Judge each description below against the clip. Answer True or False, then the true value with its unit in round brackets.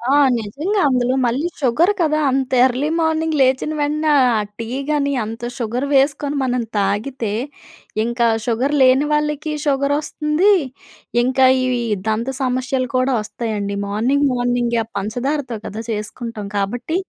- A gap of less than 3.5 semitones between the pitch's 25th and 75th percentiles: False (3.8 semitones)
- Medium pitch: False (255 Hz)